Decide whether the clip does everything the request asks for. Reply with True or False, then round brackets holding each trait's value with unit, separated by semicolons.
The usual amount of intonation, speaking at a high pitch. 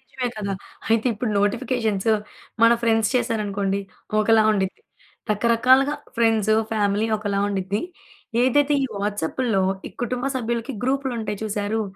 True (3.2 semitones; 225 Hz)